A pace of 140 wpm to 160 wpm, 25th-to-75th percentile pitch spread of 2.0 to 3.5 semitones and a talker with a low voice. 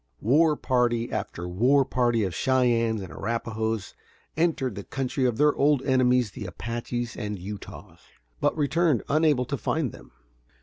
No: average, 145 wpm; average, 3.9 semitones; low, 125 Hz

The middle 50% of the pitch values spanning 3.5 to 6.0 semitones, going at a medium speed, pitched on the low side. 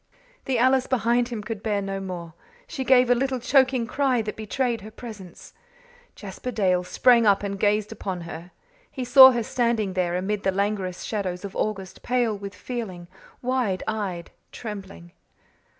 No: average, 4.2 semitones; average, 165 wpm; high, 210 Hz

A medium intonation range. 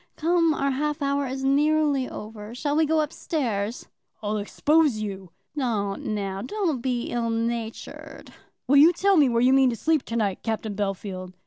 No: wide, 5.8 semitones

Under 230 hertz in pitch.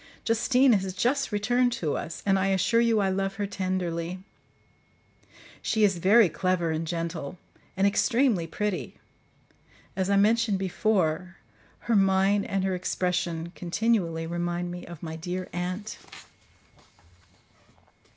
Yes: high, 190 Hz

